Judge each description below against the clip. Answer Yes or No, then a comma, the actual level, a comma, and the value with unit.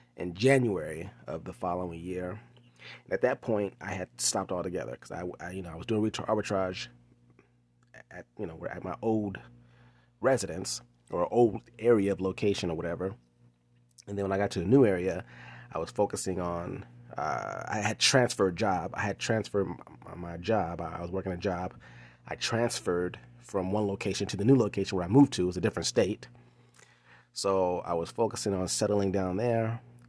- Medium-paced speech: Yes, average, 190 wpm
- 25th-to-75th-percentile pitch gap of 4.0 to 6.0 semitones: Yes, average, 4.4 semitones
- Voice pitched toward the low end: Yes, very low, 95 Hz